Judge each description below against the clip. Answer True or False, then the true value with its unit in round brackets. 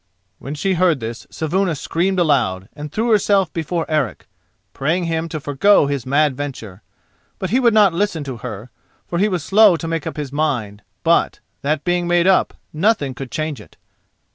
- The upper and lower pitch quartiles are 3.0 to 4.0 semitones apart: False (4.9 semitones)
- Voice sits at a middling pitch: True (155 Hz)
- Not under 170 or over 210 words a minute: True (185 wpm)